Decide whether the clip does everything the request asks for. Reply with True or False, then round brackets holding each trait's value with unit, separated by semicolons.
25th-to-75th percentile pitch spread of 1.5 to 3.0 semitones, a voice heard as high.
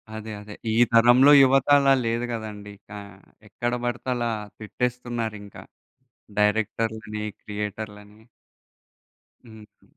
False (2.4 semitones; 110 Hz)